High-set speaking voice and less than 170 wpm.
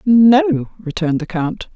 Yes: high, 195 Hz; slow, 135 wpm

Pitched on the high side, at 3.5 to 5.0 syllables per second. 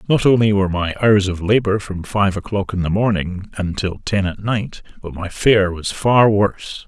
No: low, 100 Hz; 4.7 syllables/s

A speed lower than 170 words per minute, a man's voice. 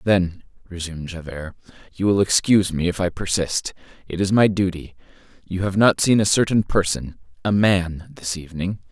Yes: average, 155 wpm; male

